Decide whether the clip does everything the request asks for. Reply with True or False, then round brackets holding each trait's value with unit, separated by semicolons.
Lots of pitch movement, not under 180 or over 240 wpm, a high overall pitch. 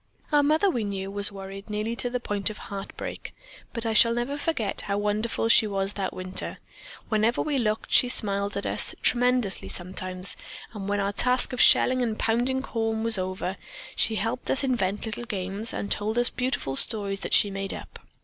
False (3.5 semitones; 190 wpm; 215 Hz)